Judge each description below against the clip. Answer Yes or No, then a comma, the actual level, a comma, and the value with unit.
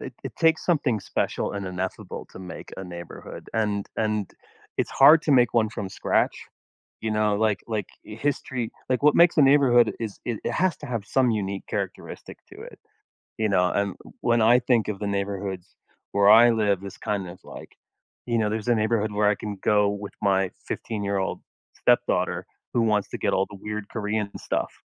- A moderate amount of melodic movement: Yes, average, 3.0 semitones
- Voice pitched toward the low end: Yes, low, 105 Hz